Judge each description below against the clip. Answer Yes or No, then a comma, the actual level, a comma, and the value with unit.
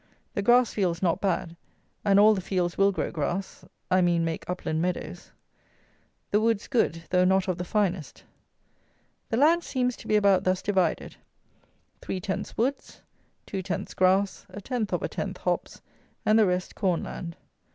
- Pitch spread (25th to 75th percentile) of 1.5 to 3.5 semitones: Yes, average, 2.9 semitones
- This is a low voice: No, high, 190 Hz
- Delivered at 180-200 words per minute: No, average, 170 wpm